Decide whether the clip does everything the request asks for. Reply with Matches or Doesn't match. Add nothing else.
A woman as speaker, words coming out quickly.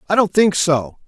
Doesn't match